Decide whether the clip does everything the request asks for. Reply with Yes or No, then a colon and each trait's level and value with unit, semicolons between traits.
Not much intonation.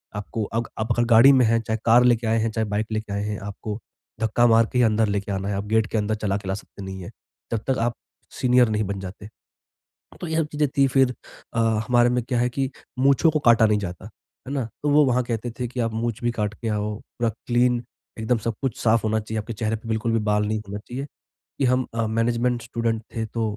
Yes: narrow, 2.3 semitones